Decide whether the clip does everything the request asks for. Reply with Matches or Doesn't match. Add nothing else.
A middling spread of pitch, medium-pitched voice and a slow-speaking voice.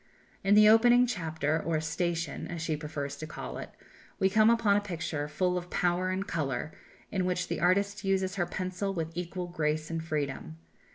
Doesn't match